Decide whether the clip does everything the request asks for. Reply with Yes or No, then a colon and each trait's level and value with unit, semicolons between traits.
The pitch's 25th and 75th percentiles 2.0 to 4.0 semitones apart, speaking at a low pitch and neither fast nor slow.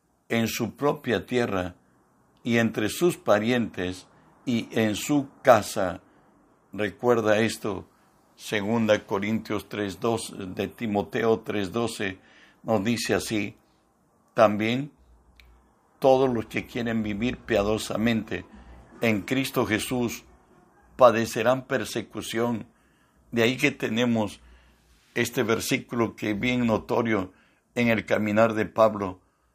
No: average, 2.8 semitones; low, 110 Hz; slow, 100 wpm